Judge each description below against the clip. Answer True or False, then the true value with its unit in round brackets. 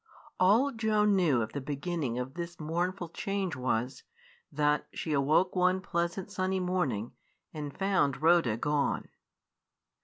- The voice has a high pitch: False (170 Hz)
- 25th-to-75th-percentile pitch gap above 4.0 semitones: True (4.8 semitones)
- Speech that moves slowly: True (130 wpm)